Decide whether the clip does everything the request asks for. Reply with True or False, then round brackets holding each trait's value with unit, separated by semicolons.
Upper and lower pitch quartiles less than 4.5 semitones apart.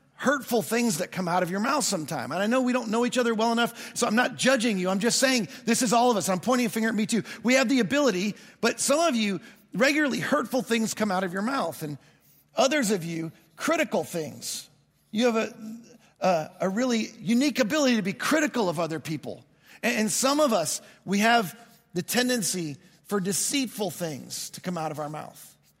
False (4.9 semitones)